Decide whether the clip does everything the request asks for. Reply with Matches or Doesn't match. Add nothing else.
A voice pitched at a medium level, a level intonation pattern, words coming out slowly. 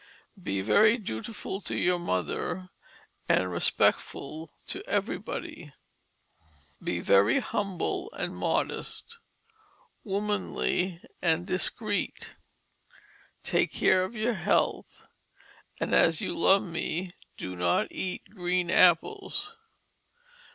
Doesn't match